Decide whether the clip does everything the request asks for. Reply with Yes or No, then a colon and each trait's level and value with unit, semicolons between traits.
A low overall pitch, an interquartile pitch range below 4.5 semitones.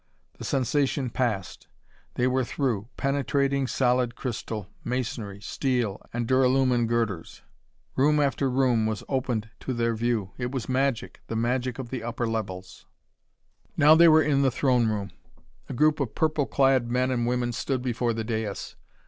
Yes: low, 125 Hz; average, 2.8 semitones